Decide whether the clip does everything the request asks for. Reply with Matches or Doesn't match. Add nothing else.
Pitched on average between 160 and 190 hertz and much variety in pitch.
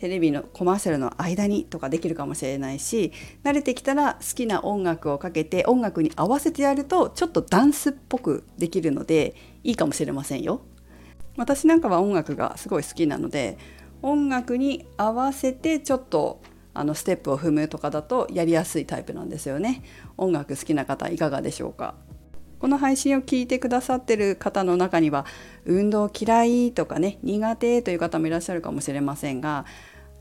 Matches